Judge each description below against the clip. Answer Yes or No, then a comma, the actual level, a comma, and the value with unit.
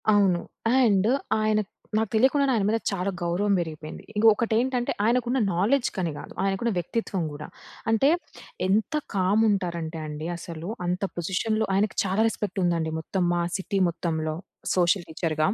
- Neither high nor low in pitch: No, high, 195 Hz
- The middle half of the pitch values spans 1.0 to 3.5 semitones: No, average, 4.2 semitones